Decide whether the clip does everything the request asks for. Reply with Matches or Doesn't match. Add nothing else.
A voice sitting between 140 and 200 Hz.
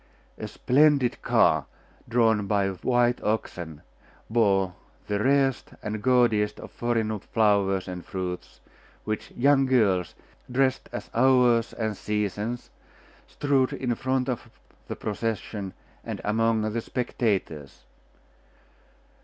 Doesn't match